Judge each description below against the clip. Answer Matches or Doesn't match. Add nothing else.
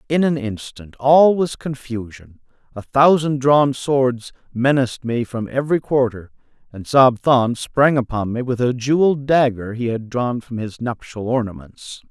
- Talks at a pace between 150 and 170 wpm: Matches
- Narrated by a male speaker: Matches